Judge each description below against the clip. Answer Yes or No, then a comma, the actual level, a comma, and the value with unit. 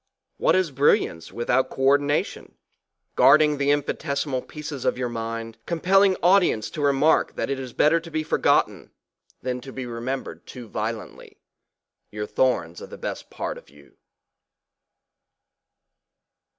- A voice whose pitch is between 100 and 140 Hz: Yes, low, 135 Hz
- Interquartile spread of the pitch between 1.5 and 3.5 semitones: No, average, 4.4 semitones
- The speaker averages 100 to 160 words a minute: Yes, average, 145 wpm